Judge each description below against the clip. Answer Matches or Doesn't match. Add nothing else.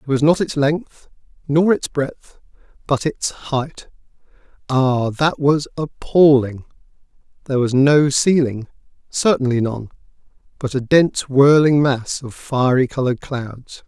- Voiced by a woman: Doesn't match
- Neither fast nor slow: Doesn't match